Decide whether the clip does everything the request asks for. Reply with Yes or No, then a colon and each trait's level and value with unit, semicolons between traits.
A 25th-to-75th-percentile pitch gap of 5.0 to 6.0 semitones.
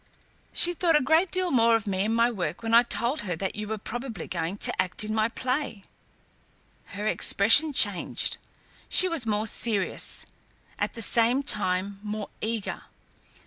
No: average, 3.8 semitones